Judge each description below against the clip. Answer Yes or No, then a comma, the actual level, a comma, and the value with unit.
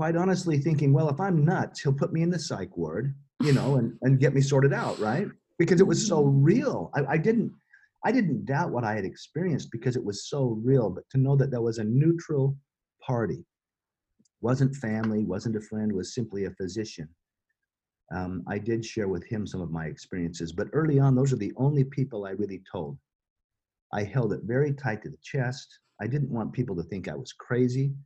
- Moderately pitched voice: No, low, 130 Hz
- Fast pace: Yes, fast, 210 wpm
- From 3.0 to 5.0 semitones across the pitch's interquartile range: No, wide, 5.6 semitones